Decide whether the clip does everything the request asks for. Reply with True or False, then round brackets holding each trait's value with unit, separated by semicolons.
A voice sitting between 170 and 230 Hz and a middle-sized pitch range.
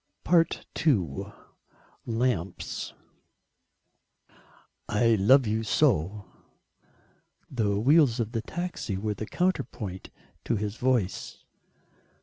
False (110 Hz; 4.4 semitones)